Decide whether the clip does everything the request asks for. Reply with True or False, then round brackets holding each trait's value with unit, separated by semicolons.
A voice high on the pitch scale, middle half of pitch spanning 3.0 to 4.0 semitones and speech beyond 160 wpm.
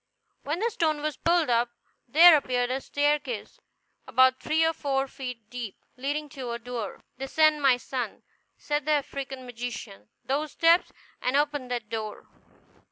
False (270 Hz; 3.5 semitones; 155 wpm)